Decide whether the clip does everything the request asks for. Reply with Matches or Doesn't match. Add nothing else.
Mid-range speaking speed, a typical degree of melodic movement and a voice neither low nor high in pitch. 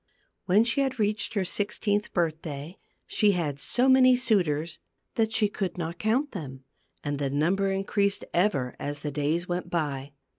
Doesn't match